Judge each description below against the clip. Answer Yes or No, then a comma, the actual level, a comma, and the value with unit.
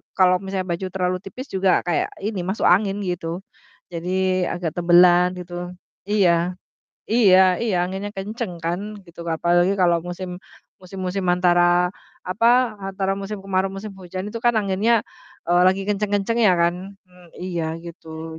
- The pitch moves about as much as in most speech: No, narrow, 2.0 semitones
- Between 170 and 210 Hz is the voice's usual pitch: Yes, medium, 185 Hz